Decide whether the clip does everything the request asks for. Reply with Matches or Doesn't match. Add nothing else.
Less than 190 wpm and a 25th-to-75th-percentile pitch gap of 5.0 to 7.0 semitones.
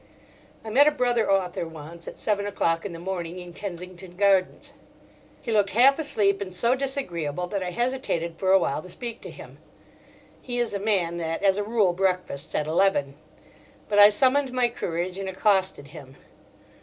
Doesn't match